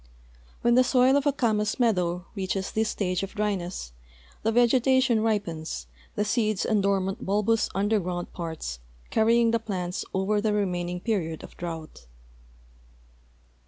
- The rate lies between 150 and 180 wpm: No, average, 140 wpm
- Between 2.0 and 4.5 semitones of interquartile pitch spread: Yes, average, 3.9 semitones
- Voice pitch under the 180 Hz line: No, high, 205 Hz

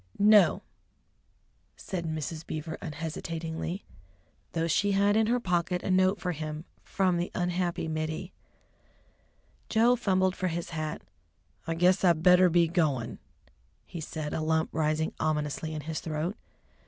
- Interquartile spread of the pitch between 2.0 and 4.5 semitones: Yes, average, 2.8 semitones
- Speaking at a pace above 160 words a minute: No, average, 140 wpm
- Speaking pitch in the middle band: Yes, medium, 170 Hz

